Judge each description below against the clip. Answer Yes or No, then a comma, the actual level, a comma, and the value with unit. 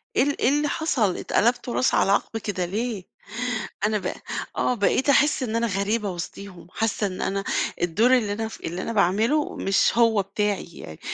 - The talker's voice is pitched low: No, high, 215 Hz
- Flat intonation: No, average, 3.5 semitones